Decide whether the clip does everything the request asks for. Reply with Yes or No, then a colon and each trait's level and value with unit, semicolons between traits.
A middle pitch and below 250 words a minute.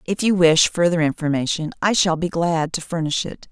Yes: medium, 165 Hz; fast, 205 wpm